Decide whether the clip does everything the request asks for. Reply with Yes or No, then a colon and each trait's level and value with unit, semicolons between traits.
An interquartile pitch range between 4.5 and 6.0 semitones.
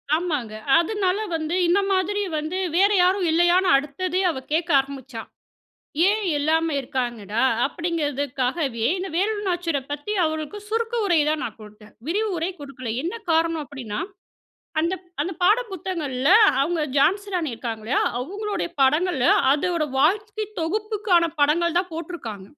Yes: average, 5.2 semitones